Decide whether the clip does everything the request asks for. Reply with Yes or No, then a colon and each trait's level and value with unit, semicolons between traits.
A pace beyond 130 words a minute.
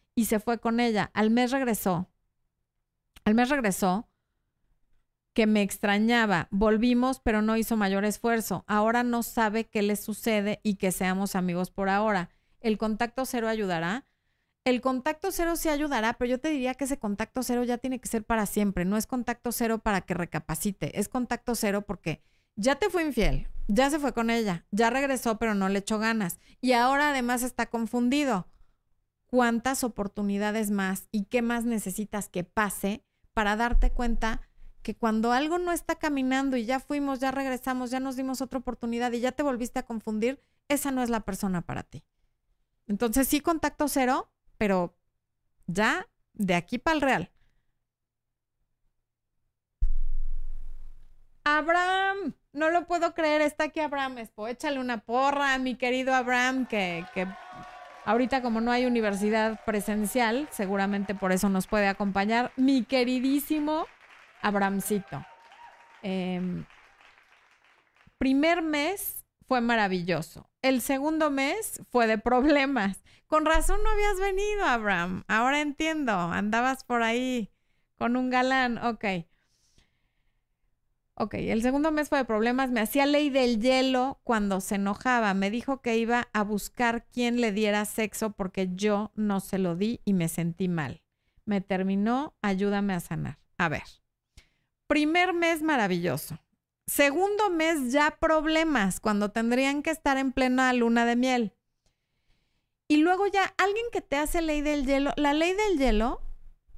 Yes: average, 150 wpm